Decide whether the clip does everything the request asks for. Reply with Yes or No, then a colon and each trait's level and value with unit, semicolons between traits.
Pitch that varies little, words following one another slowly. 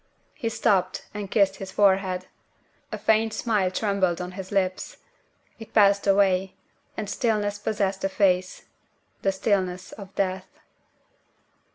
Yes: narrow, 1.8 semitones; slow, 130 wpm